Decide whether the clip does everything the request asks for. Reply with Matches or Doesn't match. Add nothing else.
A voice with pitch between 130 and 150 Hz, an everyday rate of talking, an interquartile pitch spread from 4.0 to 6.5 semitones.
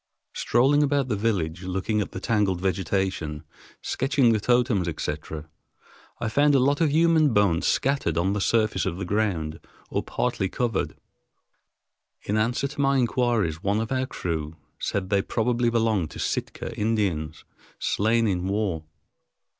Doesn't match